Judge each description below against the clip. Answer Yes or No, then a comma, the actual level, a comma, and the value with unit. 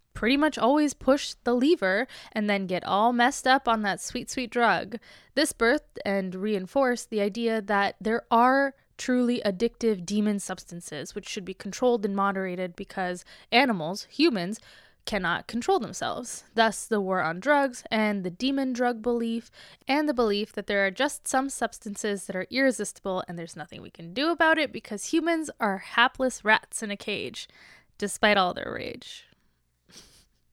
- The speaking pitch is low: No, high, 220 Hz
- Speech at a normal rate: Yes, average, 165 wpm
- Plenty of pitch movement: No, average, 4.3 semitones